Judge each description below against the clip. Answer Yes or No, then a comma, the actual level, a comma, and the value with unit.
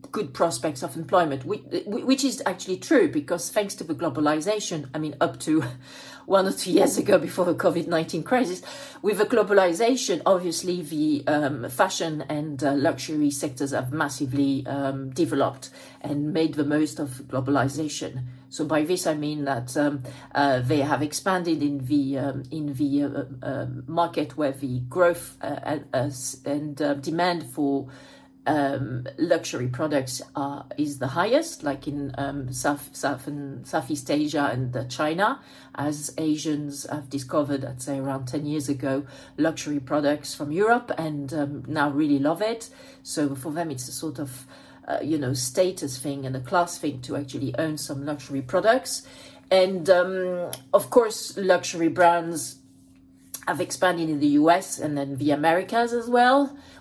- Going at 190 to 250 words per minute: No, average, 160 wpm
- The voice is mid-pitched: Yes, medium, 150 Hz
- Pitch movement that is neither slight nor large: Yes, average, 3.7 semitones